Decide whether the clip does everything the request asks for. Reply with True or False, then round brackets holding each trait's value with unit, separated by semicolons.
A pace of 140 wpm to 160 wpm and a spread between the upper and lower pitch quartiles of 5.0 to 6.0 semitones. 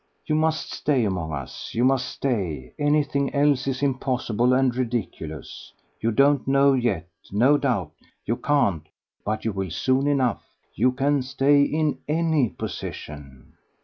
True (145 wpm; 5.4 semitones)